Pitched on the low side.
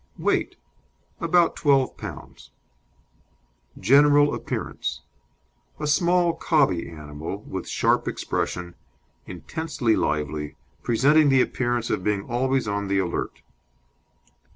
Yes: low, 120 Hz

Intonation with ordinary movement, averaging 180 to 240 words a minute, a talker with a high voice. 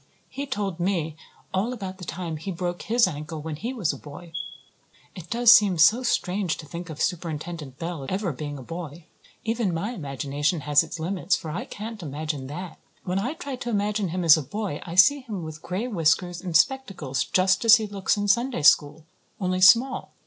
No: average, 4.8 semitones; average, 200 wpm; medium, 180 Hz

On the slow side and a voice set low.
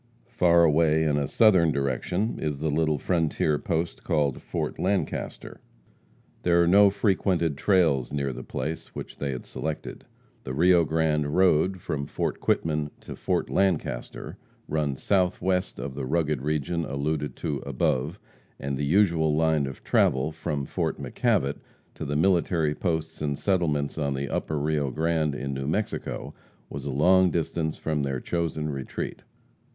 No: average, 155 wpm; very low, 75 Hz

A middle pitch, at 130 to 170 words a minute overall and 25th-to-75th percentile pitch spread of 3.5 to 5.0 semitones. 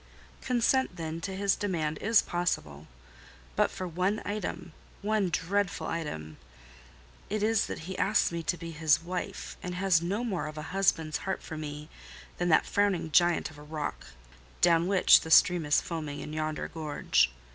Yes: medium, 170 Hz; average, 165 wpm; average, 3.8 semitones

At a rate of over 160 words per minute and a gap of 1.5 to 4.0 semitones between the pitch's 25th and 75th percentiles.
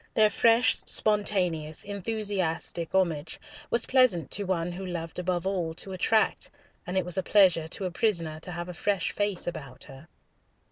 Yes: average, 170 wpm; average, 3.5 semitones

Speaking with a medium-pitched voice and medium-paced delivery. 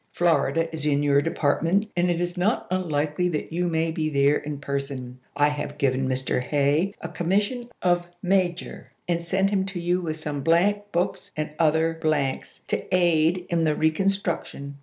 Yes: medium, 165 Hz; average, 180 wpm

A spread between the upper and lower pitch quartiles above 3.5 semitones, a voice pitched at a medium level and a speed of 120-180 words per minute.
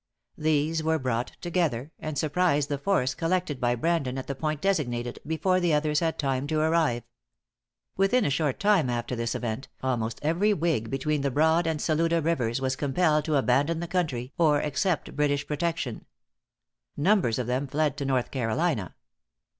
Yes: average, 4.1 semitones; medium, 150 Hz; average, 170 wpm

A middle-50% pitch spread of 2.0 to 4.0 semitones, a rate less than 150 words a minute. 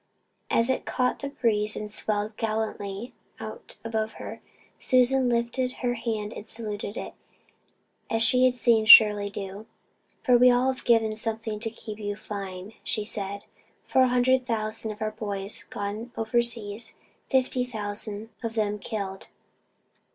Yes: narrow, 2.6 semitones; average, 140 wpm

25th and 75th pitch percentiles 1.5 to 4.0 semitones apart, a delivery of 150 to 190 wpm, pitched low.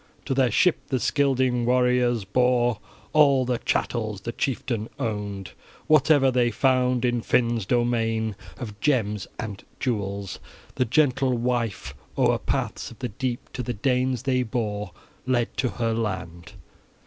No: average, 2.7 semitones; average, 140 wpm; low, 120 Hz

